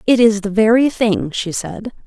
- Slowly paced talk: No, fast, 205 wpm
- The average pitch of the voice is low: No, high, 210 Hz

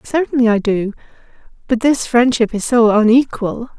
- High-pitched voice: Yes, high, 235 Hz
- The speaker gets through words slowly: Yes, slow, 125 wpm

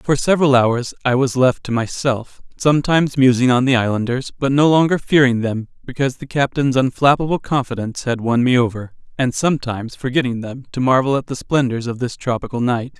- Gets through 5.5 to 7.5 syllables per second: Yes, 5.8 syllables/s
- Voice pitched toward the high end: No, low, 130 Hz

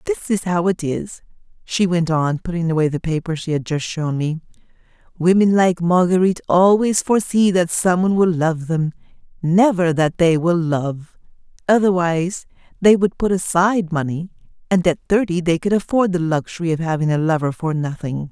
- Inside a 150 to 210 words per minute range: Yes, average, 175 wpm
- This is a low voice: No, medium, 170 Hz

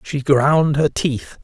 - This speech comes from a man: Yes, male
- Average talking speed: Yes, average, 170 wpm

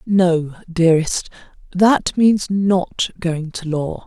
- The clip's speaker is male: No, female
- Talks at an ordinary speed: No, slow, 105 wpm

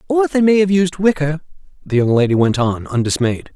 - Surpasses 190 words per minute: Yes, fast, 205 wpm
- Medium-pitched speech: Yes, medium, 155 Hz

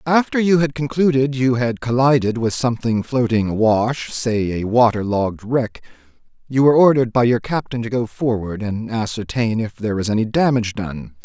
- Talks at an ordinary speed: Yes, average, 175 wpm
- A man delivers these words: Yes, male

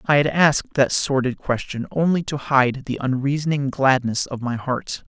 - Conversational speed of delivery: Yes, average, 175 wpm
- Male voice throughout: Yes, male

